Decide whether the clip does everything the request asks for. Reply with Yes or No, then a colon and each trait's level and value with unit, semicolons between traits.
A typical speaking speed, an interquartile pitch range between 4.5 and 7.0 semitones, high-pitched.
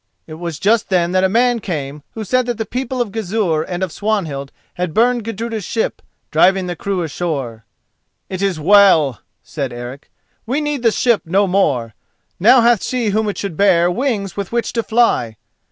Yes: average, 185 wpm; wide, 5.4 semitones; high, 195 Hz